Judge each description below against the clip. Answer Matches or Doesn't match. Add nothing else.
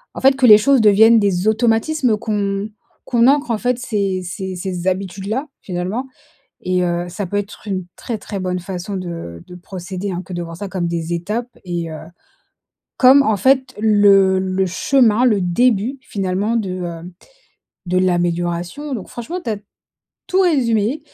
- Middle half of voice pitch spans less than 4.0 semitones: Doesn't match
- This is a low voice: Doesn't match